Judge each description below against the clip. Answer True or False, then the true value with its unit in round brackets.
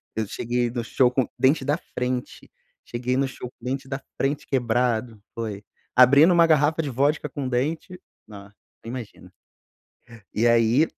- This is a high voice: False (125 Hz)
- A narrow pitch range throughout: False (3.0 semitones)